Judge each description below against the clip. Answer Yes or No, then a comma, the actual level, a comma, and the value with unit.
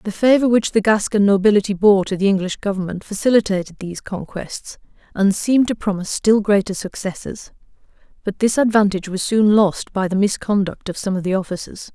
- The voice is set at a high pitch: Yes, high, 200 Hz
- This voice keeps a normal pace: Yes, average, 175 wpm